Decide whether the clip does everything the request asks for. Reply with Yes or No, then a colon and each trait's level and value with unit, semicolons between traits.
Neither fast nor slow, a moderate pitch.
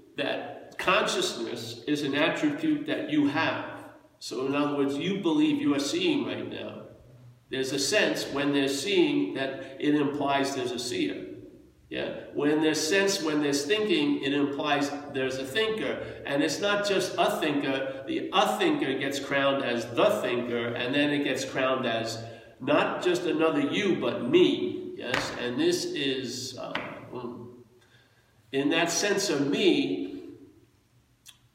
Yes: average, 150 wpm; medium, 145 Hz